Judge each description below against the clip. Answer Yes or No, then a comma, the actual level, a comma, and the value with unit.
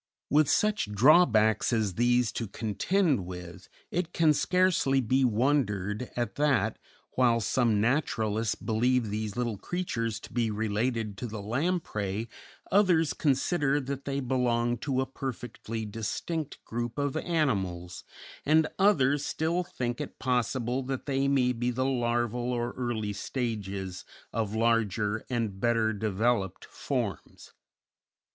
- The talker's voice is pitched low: Yes, low, 120 Hz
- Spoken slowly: Yes, slow, 130 wpm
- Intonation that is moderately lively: Yes, average, 4.0 semitones